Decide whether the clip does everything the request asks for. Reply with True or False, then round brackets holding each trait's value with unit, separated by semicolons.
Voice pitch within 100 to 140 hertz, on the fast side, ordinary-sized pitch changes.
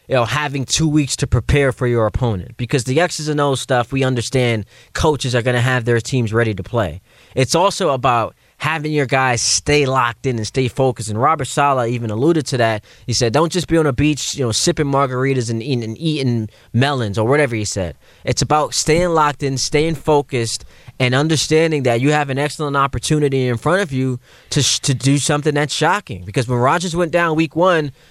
True (135 Hz; 215 wpm; 3.8 semitones)